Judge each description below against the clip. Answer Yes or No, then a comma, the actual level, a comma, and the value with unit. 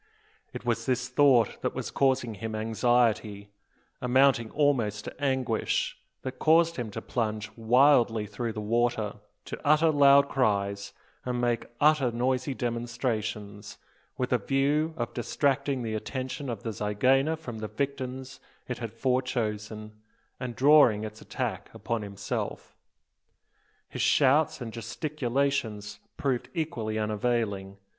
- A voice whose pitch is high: No, low, 120 Hz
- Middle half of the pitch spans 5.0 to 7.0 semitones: No, average, 3.9 semitones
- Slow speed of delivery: Yes, slow, 130 wpm